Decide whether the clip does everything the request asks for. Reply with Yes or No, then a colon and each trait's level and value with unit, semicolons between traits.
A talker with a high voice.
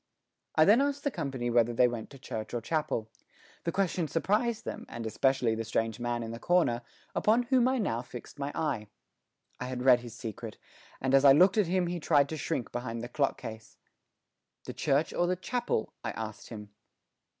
No: low, 135 Hz